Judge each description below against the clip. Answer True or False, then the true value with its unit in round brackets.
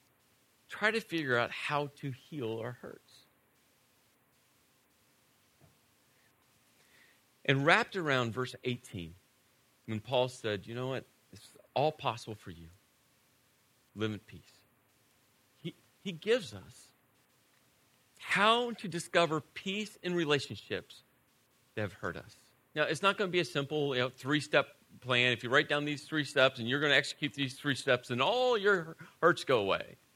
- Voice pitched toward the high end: False (135 Hz)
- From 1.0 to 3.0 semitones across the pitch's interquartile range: False (4.4 semitones)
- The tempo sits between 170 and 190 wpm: False (150 wpm)